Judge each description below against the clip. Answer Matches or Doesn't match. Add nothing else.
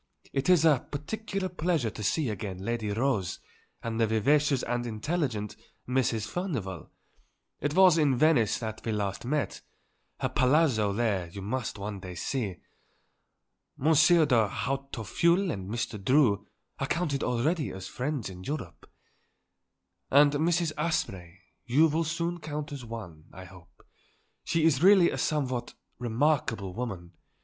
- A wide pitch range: Matches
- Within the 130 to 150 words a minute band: Matches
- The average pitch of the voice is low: Matches